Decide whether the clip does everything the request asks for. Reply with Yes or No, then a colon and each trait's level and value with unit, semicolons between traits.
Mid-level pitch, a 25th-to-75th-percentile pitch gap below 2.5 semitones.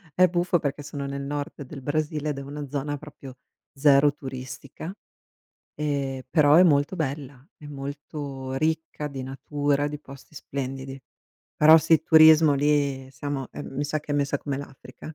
Yes: medium, 145 Hz; narrow, 1.8 semitones